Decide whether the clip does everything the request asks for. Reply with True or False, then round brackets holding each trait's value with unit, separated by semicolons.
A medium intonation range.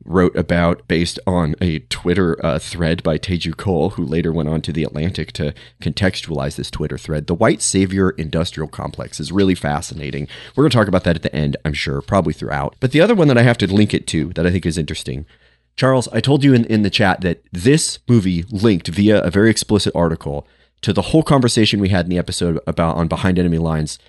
True (4.6 semitones)